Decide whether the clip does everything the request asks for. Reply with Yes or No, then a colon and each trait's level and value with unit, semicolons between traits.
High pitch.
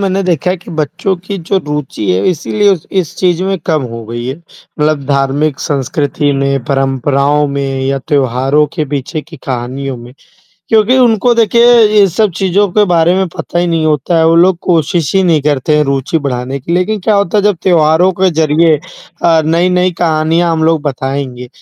No: medium, 155 Hz